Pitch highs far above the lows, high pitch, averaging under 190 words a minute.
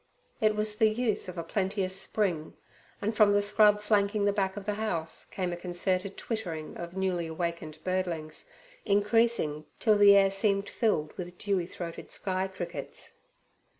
No: average, 3.1 semitones; high, 195 Hz; average, 160 wpm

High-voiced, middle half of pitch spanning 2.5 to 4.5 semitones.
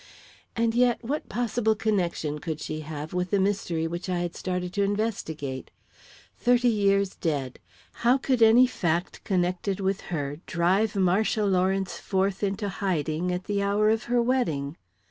Yes: high, 195 Hz; average, 4.1 semitones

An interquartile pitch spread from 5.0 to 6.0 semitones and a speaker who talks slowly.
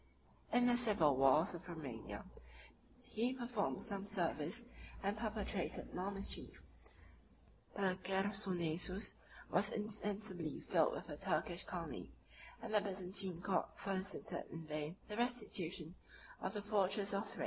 No: average, 3.1 semitones; slow, 130 wpm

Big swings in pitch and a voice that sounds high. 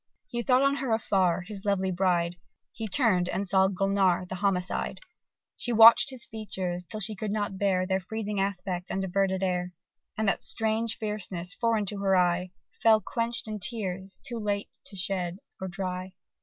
No: average, 2.9 semitones; high, 195 Hz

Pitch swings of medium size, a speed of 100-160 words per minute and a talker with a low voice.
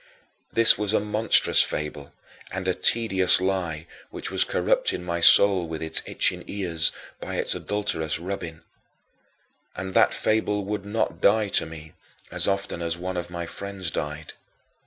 Yes: average, 3.6 semitones; average, 155 wpm; very low, 95 Hz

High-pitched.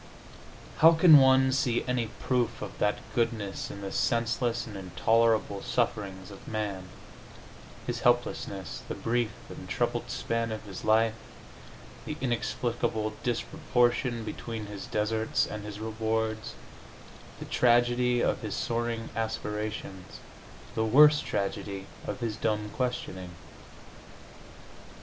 No: low, 115 Hz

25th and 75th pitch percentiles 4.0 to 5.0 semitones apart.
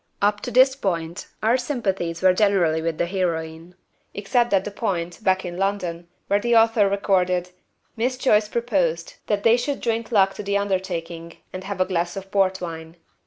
No: average, 3.6 semitones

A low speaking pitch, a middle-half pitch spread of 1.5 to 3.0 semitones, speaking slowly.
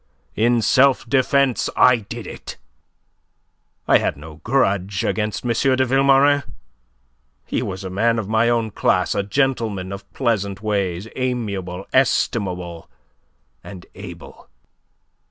No: low, 110 Hz; average, 4.8 semitones; slow, 120 wpm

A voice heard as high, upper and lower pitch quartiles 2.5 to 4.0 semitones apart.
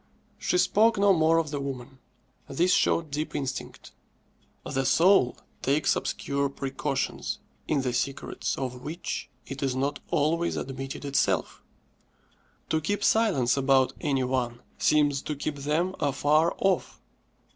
No: medium, 145 Hz; average, 3.2 semitones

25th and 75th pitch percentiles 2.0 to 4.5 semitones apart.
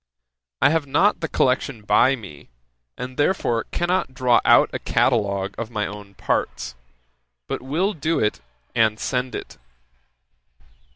No: wide, 5.5 semitones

